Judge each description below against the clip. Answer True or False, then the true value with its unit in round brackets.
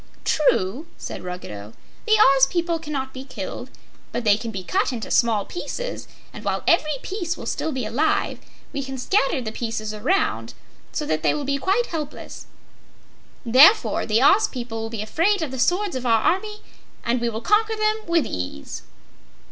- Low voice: False (270 Hz)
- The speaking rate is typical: True (180 wpm)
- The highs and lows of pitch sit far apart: True (7.3 semitones)